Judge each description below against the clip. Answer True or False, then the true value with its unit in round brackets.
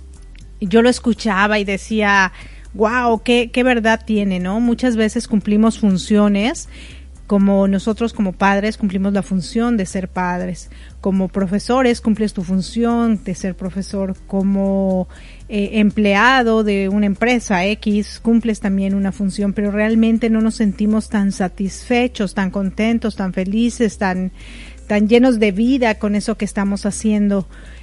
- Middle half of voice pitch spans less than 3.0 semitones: True (2.4 semitones)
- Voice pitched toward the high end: True (205 Hz)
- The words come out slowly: False (140 wpm)